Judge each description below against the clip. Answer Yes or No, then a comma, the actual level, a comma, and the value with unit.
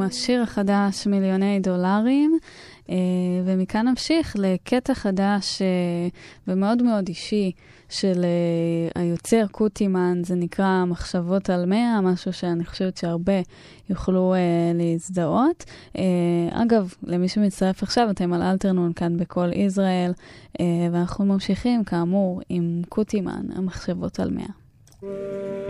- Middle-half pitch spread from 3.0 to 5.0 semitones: No, narrow, 2.4 semitones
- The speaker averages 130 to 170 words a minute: No, slow, 100 wpm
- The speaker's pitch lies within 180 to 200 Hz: Yes, high, 190 Hz